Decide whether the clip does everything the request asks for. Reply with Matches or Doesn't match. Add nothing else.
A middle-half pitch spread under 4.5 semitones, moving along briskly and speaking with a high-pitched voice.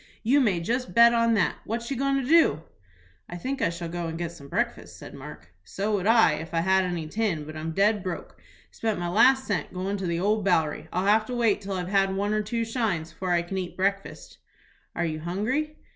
Doesn't match